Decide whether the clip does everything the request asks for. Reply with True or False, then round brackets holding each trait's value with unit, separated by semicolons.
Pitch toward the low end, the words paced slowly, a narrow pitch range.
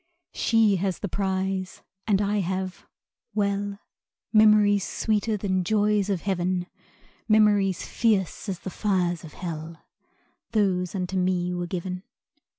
False (190 Hz; 125 wpm; 2.2 semitones)